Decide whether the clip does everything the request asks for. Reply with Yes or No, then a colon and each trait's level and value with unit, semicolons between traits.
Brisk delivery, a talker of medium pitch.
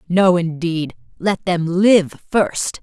No: slow, 130 wpm; medium, 175 Hz